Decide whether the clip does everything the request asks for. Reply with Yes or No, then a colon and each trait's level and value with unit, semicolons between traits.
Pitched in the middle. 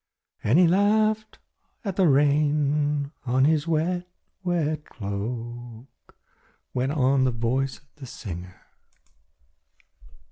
Yes: medium, 145 Hz